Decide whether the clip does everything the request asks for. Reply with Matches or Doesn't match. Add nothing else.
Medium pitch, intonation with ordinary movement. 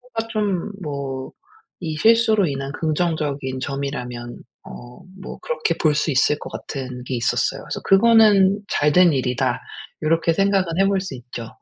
Doesn't match